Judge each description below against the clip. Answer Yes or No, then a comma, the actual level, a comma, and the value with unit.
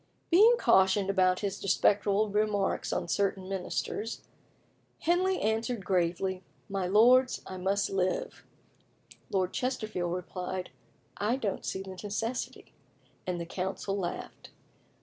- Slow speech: Yes, slow, 115 wpm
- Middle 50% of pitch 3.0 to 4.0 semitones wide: No, narrow, 2.6 semitones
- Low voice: No, high, 195 Hz